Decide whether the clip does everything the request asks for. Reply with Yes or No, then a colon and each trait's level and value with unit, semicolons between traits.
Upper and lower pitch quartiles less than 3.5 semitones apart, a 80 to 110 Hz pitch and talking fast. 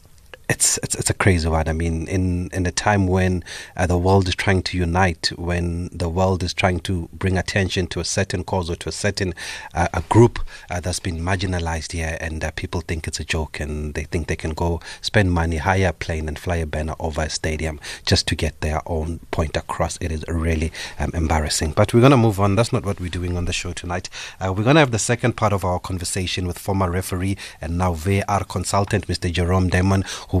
Yes: narrow, 2.6 semitones; very low, 90 Hz; fast, 235 wpm